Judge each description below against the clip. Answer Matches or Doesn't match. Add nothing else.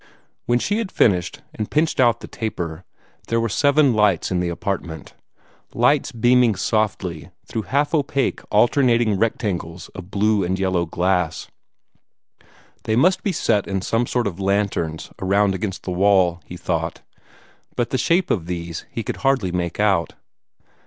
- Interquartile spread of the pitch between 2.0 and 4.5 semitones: Doesn't match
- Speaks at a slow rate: Doesn't match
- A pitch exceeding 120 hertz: Doesn't match